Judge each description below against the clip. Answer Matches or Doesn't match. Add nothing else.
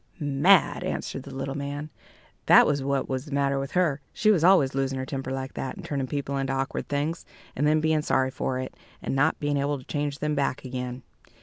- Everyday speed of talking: Doesn't match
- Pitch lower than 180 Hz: Matches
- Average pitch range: Doesn't match